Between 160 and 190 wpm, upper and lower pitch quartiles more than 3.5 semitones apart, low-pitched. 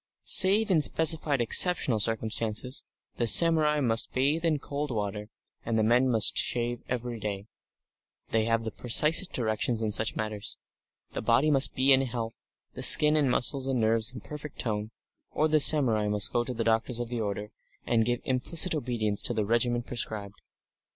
Yes: average, 175 wpm; average, 4.3 semitones; low, 120 Hz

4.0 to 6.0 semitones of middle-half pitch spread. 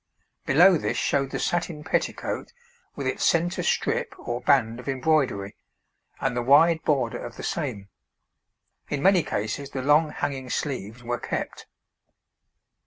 Yes: average, 4.4 semitones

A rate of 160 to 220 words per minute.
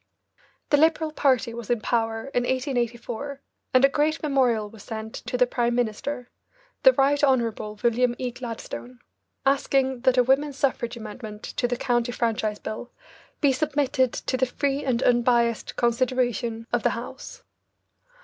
No: average, 150 wpm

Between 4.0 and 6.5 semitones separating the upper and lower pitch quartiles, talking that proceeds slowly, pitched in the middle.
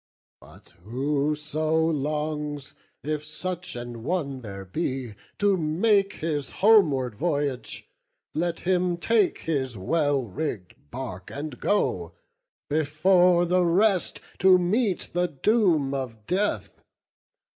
Yes: average, 5.0 semitones; slow, 110 wpm; medium, 155 Hz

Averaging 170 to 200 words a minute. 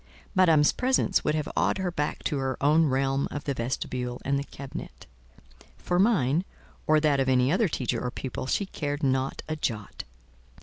Yes: average, 175 wpm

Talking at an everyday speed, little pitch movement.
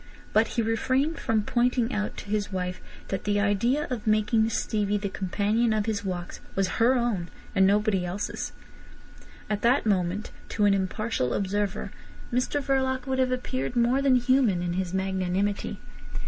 No: average, 160 wpm; average, 3.8 semitones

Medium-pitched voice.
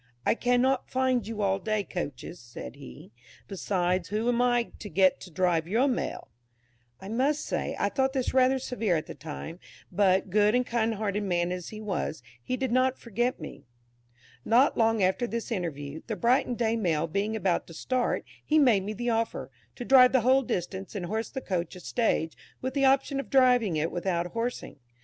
No: high, 215 Hz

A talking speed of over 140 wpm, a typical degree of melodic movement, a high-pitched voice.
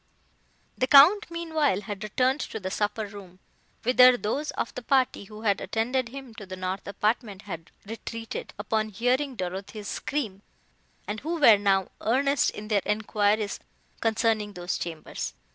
Yes: average, 150 wpm; average, 4.0 semitones; high, 220 Hz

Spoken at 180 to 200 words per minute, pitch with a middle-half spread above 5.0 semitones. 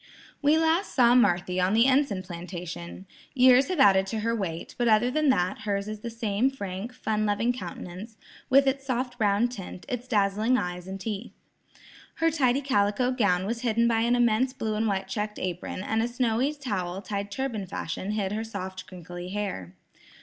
No: average, 185 wpm; average, 4.5 semitones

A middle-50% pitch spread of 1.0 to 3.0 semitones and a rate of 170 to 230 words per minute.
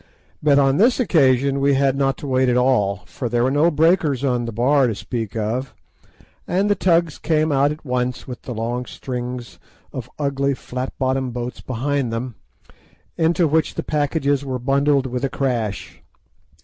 Yes: average, 2.7 semitones; average, 175 wpm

